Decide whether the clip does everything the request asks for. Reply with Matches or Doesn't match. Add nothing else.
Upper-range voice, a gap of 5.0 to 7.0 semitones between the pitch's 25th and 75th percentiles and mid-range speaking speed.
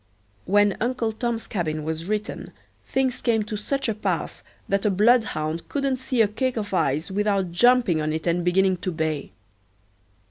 Matches